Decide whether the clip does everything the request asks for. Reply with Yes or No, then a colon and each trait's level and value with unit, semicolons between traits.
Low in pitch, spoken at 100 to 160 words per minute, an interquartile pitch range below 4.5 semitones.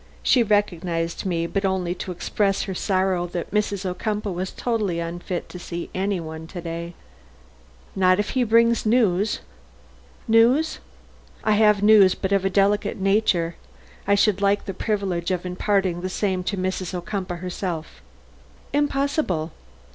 No: high, 190 Hz; average, 145 wpm; average, 2.8 semitones